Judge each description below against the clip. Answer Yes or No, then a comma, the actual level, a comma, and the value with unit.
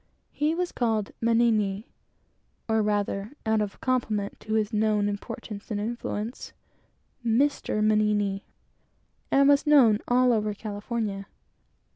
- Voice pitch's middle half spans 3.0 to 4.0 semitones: No, narrow, 2.5 semitones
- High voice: Yes, high, 215 Hz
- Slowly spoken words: Yes, slow, 115 wpm